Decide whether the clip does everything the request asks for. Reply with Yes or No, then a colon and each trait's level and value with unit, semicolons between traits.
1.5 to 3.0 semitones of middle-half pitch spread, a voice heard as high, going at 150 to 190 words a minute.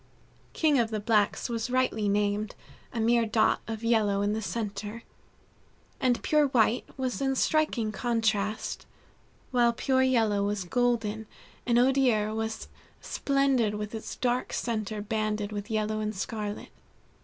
No: narrow, 2.6 semitones; high, 220 Hz; average, 140 wpm